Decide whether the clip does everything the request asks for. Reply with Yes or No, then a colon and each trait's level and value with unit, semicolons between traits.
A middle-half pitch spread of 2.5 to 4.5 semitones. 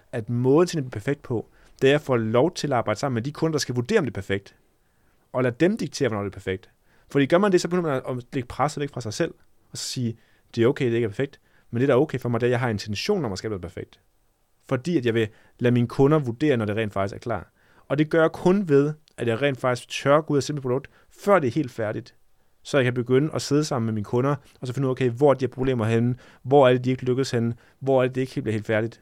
Yes: average, 3.9 semitones